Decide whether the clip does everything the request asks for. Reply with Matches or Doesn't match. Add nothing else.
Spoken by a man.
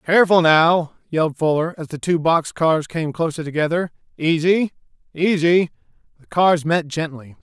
Matches